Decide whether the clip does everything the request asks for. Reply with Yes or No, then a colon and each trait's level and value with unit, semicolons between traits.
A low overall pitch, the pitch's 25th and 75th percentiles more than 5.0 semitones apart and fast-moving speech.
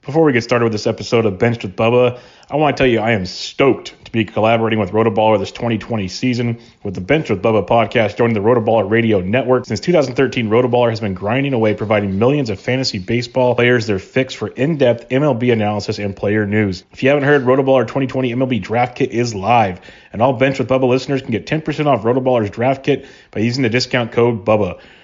No: low, 120 Hz; average, 3.1 semitones; fast, 215 wpm